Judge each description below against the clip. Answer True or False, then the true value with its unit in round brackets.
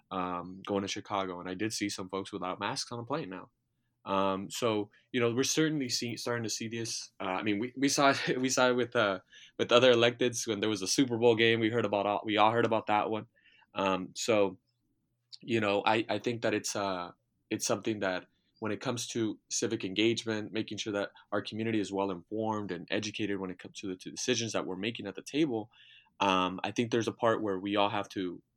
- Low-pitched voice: True (110 Hz)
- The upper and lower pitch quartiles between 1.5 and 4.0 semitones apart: True (3.3 semitones)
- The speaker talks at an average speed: False (235 wpm)